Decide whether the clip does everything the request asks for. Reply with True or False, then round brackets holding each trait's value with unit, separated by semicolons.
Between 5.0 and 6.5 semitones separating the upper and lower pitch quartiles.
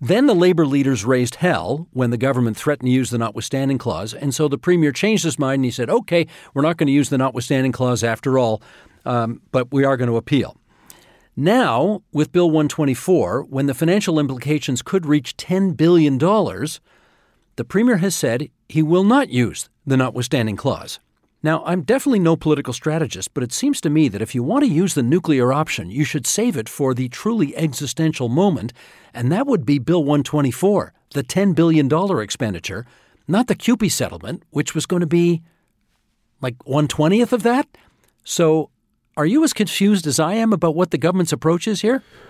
True (5.5 semitones)